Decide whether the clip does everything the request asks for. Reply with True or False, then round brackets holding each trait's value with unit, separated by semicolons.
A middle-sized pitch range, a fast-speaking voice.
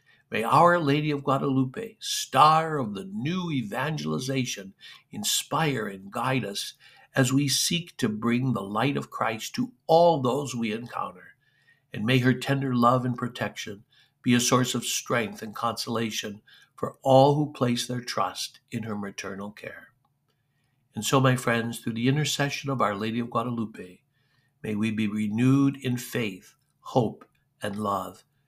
False (3.8 semitones; 155 wpm)